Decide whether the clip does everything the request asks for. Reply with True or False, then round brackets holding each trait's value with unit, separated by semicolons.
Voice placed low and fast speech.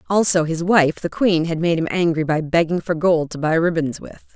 False (165 Hz; 235 wpm)